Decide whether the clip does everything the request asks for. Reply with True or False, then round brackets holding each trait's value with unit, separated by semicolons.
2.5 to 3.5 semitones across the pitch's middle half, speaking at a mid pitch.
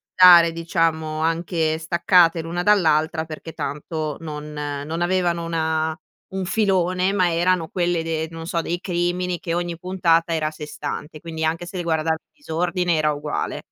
False (1.8 semitones; 165 Hz)